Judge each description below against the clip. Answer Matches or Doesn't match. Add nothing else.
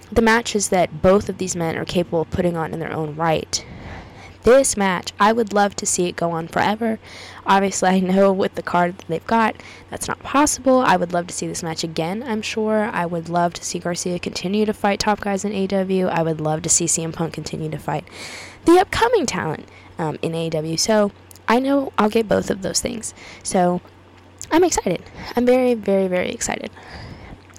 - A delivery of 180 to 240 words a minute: Matches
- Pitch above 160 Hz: Matches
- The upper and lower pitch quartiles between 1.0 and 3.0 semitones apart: Doesn't match